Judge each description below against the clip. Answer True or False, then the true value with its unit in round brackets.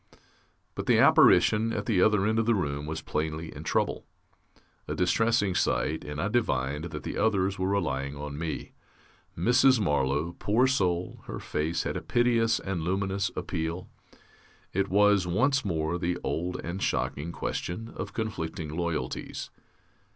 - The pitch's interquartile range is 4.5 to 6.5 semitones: True (5.0 semitones)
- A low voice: True (90 Hz)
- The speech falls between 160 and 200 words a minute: False (150 wpm)